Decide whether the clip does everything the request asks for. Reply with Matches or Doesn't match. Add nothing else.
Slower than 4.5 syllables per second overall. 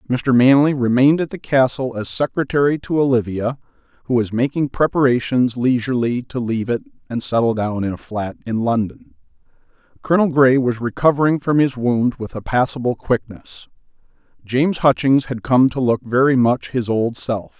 Doesn't match